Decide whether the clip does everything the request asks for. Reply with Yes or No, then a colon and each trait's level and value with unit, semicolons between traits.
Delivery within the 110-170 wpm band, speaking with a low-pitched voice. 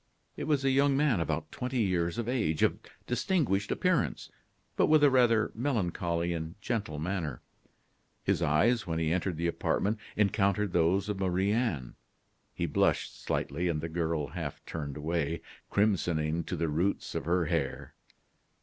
Yes: average, 160 wpm; very low, 90 Hz